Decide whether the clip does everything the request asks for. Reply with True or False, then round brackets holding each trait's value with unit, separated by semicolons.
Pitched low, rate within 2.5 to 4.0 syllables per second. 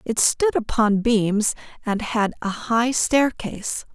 False (225 Hz; 3.5 syllables/s)